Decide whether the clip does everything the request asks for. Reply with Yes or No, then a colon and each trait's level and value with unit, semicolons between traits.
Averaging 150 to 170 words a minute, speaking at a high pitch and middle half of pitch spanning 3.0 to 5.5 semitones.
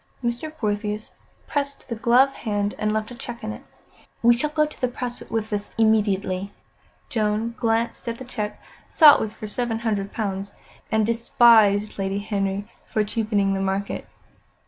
No: average, 165 wpm; high, 220 Hz; narrow, 2.5 semitones